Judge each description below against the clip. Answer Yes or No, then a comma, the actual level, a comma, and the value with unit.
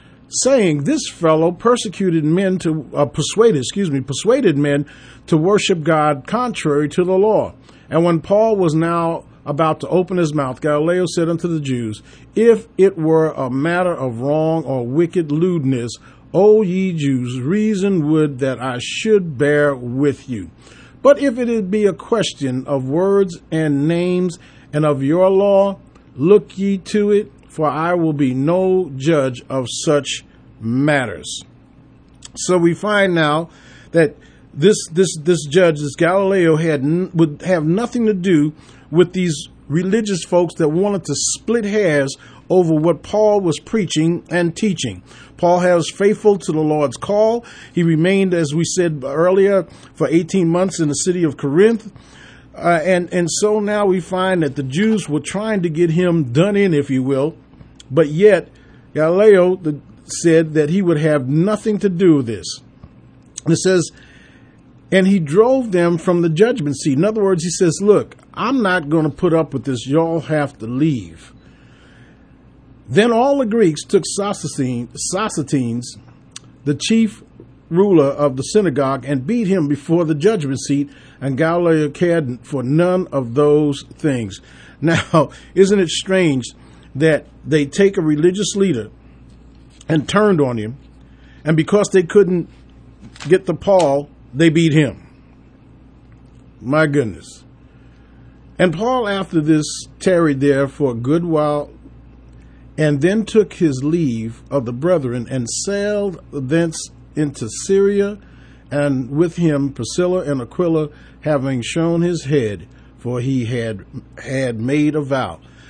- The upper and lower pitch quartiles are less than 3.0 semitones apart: No, average, 4.9 semitones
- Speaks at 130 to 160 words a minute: Yes, average, 150 wpm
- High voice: No, medium, 160 Hz